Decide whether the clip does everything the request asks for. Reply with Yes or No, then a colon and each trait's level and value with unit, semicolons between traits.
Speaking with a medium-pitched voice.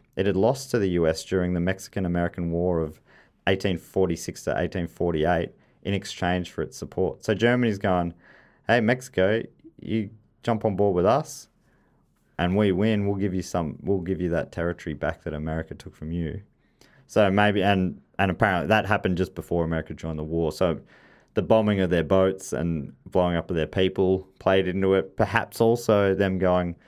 No: very low, 95 Hz